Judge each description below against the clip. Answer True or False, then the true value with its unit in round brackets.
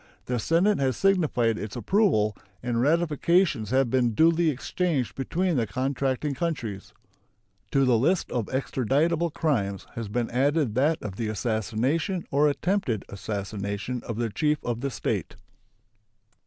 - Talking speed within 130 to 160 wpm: True (140 wpm)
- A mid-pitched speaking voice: False (130 Hz)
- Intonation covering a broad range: True (6.0 semitones)